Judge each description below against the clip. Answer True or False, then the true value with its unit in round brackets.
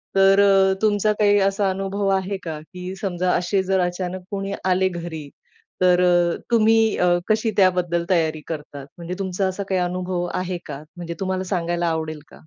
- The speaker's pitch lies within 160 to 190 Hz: True (185 Hz)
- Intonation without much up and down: True (2.0 semitones)